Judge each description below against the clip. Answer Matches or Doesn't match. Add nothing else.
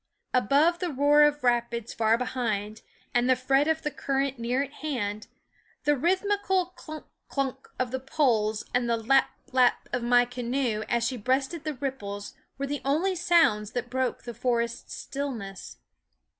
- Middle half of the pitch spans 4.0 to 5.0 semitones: Doesn't match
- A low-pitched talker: Doesn't match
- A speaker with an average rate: Matches